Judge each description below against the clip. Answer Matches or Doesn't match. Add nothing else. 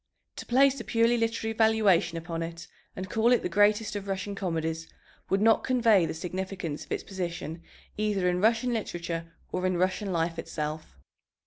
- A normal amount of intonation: Matches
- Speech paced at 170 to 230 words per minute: Matches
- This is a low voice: Doesn't match